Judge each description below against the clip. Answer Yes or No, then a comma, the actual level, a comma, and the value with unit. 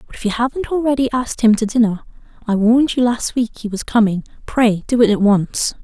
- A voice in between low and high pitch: No, high, 230 Hz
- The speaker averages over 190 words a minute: Yes, fast, 205 wpm